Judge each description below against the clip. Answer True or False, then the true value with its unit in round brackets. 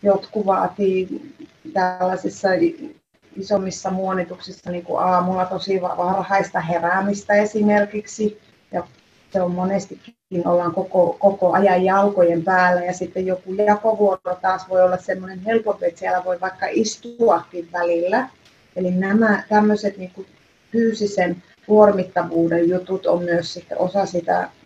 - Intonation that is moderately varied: False (2.2 semitones)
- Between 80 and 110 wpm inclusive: False (120 wpm)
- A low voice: False (185 Hz)